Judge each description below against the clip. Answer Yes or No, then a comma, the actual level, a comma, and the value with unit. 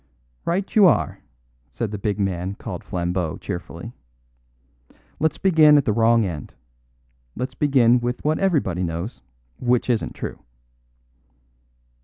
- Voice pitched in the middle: No, low, 115 Hz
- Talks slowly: Yes, slow, 125 wpm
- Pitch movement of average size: No, wide, 8.0 semitones